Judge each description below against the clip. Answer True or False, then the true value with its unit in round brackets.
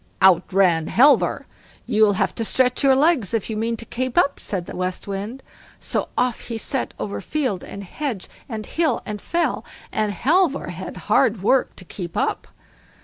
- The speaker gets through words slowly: False (180 wpm)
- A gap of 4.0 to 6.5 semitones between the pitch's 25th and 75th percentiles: True (5.2 semitones)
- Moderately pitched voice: False (225 Hz)